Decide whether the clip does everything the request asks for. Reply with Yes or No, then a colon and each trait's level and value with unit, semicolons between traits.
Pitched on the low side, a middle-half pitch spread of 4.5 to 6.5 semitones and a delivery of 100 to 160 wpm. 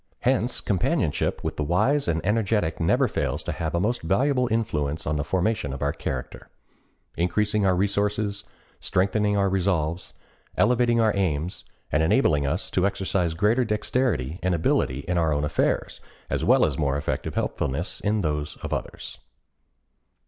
Yes: very low, 95 Hz; average, 5.2 semitones; average, 150 wpm